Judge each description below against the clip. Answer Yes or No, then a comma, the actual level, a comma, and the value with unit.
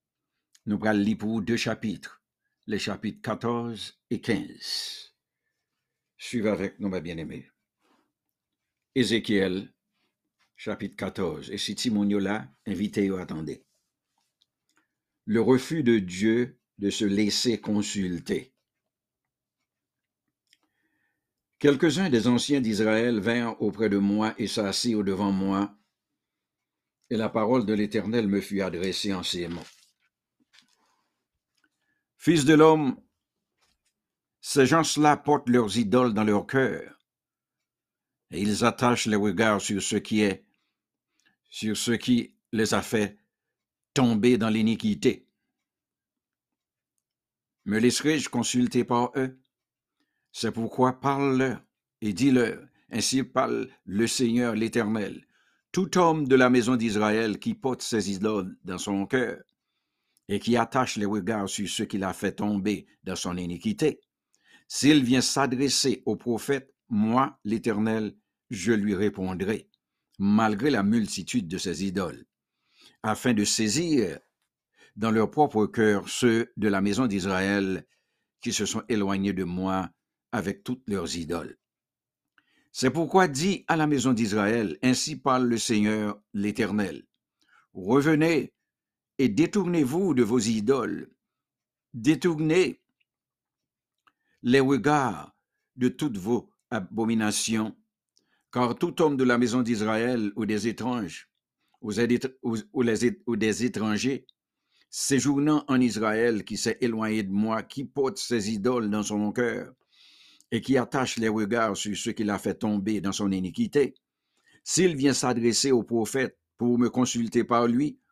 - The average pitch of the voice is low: Yes, low, 115 Hz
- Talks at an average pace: No, slow, 120 wpm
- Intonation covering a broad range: No, average, 3.5 semitones